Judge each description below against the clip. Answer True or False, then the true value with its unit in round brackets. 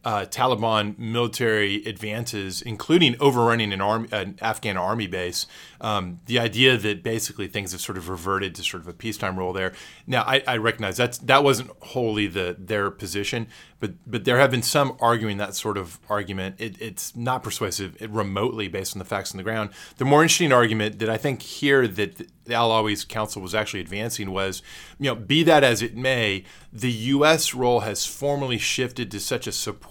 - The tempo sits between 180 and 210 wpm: True (195 wpm)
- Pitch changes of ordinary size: True (3.5 semitones)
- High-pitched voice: False (110 Hz)